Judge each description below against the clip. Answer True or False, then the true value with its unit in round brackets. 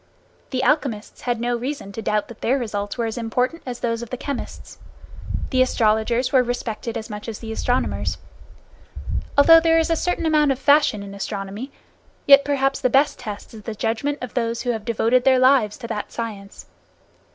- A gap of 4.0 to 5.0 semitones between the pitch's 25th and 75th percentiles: False (3.5 semitones)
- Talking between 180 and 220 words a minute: True (190 wpm)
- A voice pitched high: True (240 Hz)